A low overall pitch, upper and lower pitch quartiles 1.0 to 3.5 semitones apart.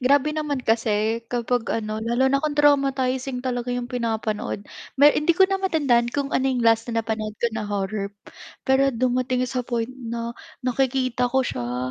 No: high, 245 Hz; average, 2.8 semitones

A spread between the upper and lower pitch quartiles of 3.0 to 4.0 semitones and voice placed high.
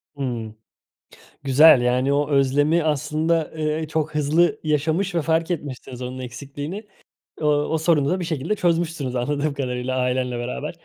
No: average, 3.7 semitones; medium, 145 Hz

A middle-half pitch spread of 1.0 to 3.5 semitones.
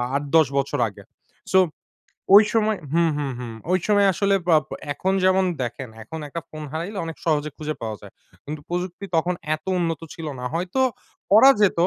No: average, 4.2 semitones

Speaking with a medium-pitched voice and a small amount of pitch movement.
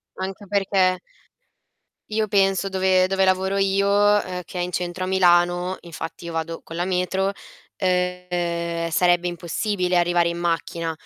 Yes: medium, 180 Hz; narrow, 1.7 semitones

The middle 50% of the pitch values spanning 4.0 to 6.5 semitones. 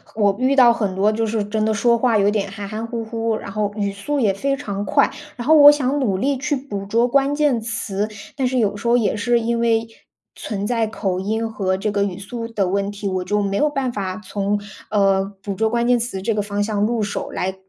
No: average, 3.0 semitones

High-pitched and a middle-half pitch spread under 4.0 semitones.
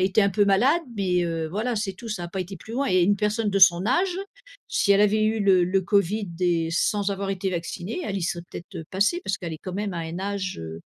Yes: high, 195 Hz; average, 3.0 semitones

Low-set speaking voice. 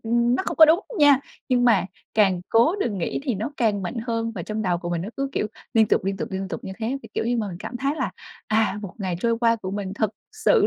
No: high, 220 Hz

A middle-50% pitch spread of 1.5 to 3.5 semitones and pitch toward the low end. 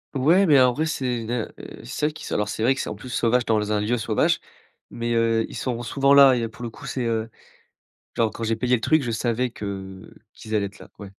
Yes: narrow, 2.6 semitones; low, 115 Hz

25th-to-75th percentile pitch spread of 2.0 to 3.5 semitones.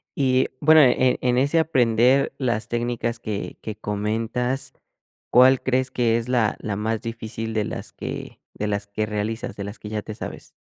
Yes: average, 2.9 semitones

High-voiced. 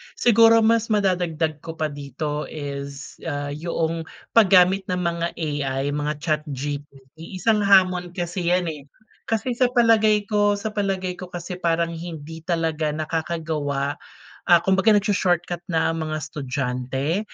No: medium, 165 Hz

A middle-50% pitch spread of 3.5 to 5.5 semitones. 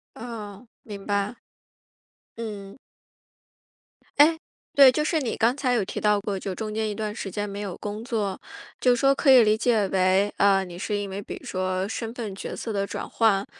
No: average, 2.8 semitones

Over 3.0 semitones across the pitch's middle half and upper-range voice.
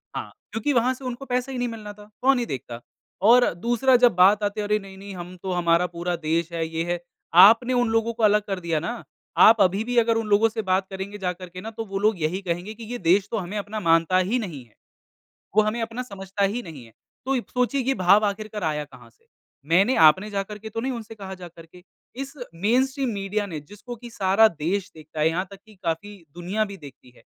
Yes: average, 4.5 semitones; high, 205 Hz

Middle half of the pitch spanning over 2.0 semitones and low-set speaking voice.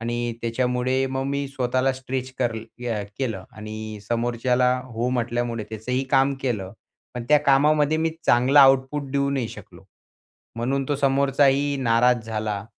Yes: average, 2.7 semitones; low, 125 Hz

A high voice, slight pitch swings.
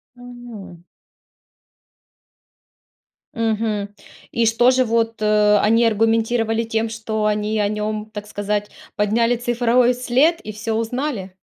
Yes: high, 225 Hz; narrow, 2.0 semitones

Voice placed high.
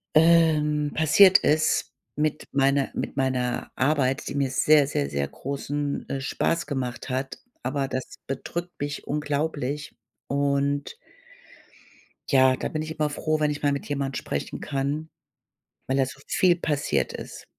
No: medium, 140 Hz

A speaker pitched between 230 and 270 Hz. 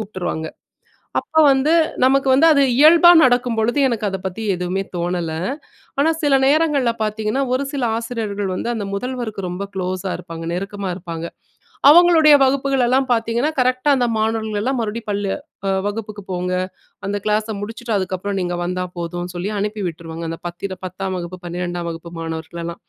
No: high, 205 Hz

